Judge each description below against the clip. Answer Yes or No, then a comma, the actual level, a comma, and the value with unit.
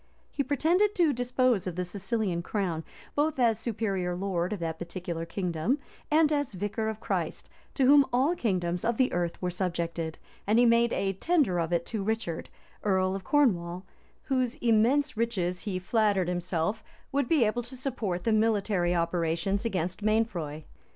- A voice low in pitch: No, high, 205 Hz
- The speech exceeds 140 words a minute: Yes, average, 165 wpm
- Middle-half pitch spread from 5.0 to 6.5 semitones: Yes, wide, 5.4 semitones